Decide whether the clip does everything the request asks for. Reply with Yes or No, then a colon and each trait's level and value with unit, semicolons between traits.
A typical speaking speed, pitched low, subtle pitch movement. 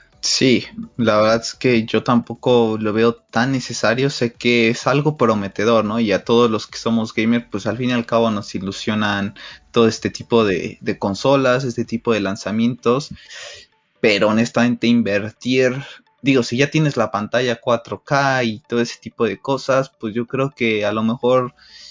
Yes: average, 180 wpm; low, 115 Hz; narrow, 2.2 semitones